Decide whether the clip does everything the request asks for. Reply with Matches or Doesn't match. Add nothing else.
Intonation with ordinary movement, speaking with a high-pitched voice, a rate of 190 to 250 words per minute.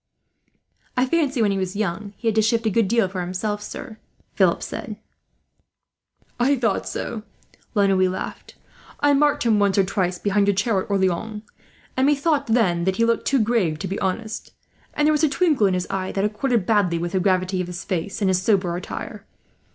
Matches